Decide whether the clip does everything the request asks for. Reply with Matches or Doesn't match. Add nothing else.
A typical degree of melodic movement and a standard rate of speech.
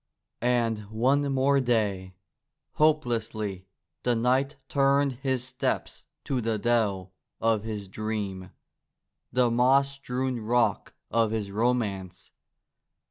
Doesn't match